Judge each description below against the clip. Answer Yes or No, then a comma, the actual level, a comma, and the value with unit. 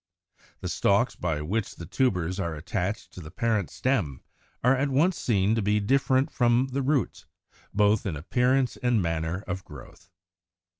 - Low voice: Yes, low, 105 Hz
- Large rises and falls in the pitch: Yes, wide, 6.3 semitones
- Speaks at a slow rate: No, average, 160 wpm